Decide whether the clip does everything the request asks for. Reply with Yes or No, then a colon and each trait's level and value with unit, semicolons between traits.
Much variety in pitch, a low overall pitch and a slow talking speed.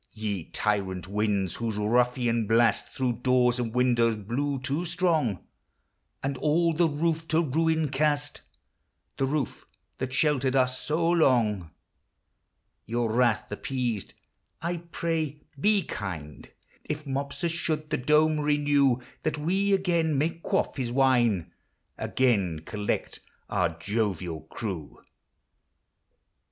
Yes: wide, 5.8 semitones; low, 130 Hz; slow, 120 wpm